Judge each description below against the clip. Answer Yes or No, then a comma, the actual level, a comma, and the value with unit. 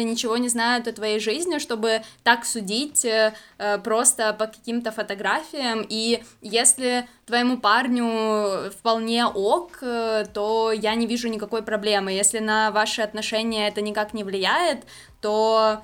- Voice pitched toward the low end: No, high, 220 Hz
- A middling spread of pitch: No, narrow, 1.6 semitones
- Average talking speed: Yes, average, 130 wpm